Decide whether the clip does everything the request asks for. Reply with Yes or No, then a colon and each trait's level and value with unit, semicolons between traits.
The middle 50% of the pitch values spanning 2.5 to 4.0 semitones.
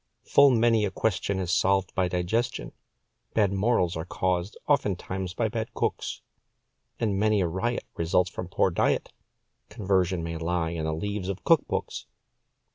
Yes: average, 3.4 semitones